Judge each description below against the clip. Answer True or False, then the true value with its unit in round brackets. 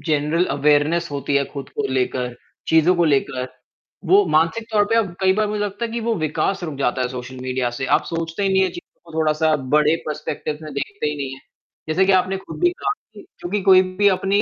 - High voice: False (160 Hz)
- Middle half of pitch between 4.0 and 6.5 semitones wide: True (5.3 semitones)